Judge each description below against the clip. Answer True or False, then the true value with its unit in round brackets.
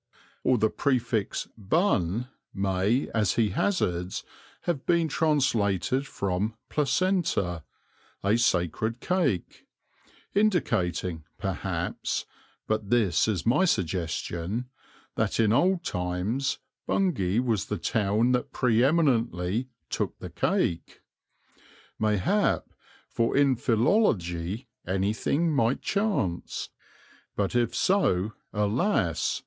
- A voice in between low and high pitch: False (115 Hz)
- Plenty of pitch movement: True (6.6 semitones)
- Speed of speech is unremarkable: False (100 wpm)